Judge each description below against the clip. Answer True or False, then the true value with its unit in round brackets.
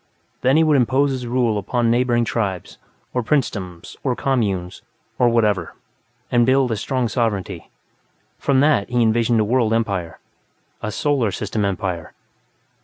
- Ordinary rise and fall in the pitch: True (3.9 semitones)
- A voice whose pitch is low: True (115 Hz)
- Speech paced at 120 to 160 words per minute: True (145 wpm)